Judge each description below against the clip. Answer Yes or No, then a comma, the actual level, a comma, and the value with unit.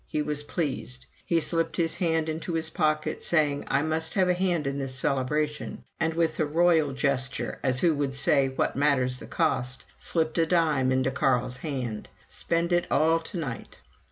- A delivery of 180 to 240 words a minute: Yes, average, 185 wpm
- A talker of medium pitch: Yes, medium, 150 Hz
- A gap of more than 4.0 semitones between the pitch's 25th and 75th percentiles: No, average, 3.4 semitones